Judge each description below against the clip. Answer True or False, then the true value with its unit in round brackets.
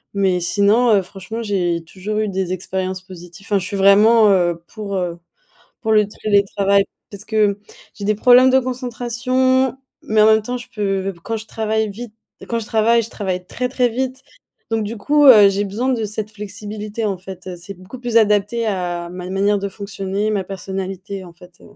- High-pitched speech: True (205 Hz)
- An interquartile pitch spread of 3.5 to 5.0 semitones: False (2.8 semitones)